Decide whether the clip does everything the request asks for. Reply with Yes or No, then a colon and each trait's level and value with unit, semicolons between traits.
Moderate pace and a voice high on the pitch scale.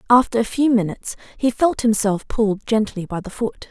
Yes: average, 195 wpm; high, 225 Hz